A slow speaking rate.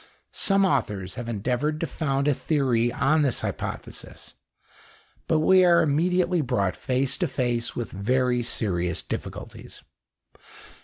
Yes: slow, 125 wpm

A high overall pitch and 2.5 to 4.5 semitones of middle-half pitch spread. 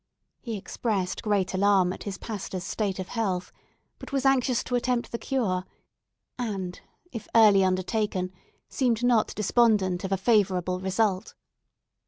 Yes: high, 205 Hz; average, 3.6 semitones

